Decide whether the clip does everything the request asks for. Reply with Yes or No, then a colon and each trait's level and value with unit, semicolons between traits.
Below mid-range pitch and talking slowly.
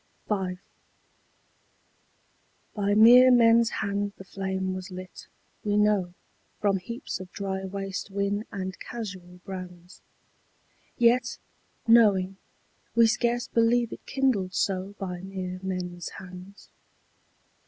No: high, 195 Hz; slow, 110 wpm